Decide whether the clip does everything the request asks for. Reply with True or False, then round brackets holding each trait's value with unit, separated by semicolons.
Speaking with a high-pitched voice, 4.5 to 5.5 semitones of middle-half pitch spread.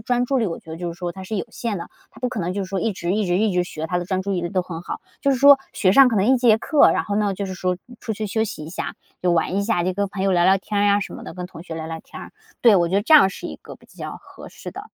False (195 Hz; 3.8 semitones)